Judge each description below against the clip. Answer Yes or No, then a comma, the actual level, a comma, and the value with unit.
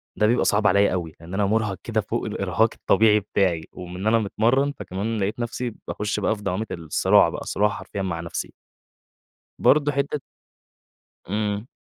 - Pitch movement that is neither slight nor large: Yes, average, 3.0 semitones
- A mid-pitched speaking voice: No, low, 105 Hz